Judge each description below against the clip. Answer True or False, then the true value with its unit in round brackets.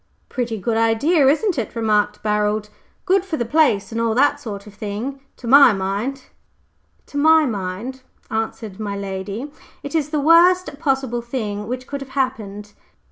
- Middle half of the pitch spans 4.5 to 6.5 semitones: True (5.2 semitones)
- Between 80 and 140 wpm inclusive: False (150 wpm)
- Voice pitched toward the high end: True (235 Hz)